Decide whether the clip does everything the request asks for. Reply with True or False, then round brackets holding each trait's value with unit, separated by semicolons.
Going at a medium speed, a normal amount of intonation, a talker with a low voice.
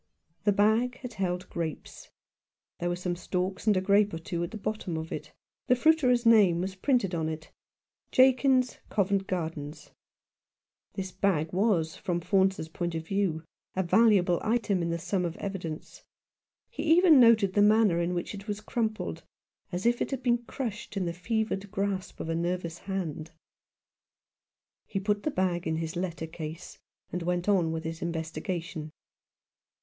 False (170 wpm; 4.0 semitones; 190 Hz)